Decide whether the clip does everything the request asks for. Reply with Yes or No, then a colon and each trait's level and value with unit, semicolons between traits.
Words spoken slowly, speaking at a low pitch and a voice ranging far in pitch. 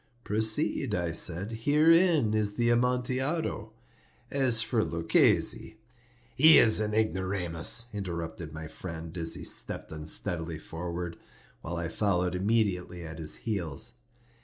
Yes: slow, 120 wpm; very low, 95 Hz; wide, 5.7 semitones